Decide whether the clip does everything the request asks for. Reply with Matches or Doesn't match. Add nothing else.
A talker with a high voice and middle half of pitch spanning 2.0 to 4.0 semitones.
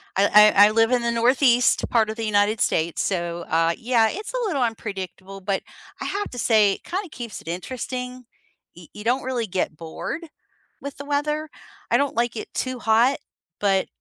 Doesn't match